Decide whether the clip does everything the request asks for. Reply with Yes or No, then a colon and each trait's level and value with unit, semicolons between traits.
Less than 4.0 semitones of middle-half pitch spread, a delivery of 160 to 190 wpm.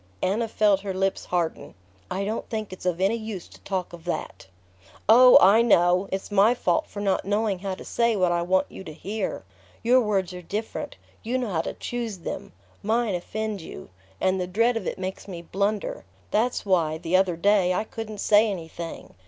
No: average, 3.2 semitones; average, 200 wpm